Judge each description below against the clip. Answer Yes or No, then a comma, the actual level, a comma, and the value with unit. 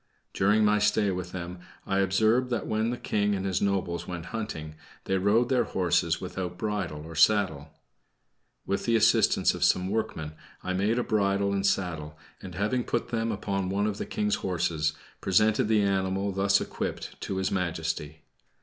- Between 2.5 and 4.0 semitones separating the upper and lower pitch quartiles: Yes, average, 2.9 semitones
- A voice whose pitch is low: Yes, very low, 95 Hz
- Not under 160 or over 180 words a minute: Yes, average, 175 wpm